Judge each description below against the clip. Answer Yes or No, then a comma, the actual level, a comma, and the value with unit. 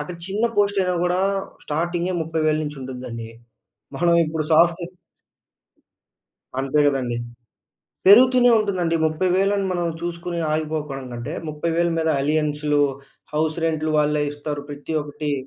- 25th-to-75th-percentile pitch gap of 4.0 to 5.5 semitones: No, average, 3.0 semitones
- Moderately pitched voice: Yes, medium, 155 Hz